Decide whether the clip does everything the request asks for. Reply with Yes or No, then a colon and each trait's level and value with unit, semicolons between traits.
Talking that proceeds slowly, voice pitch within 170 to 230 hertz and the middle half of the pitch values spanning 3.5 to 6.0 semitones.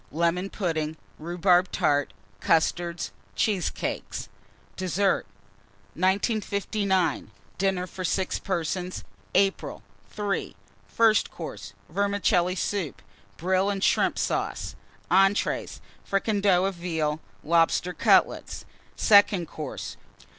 No: slow, 90 wpm; medium, 185 Hz; average, 2.7 semitones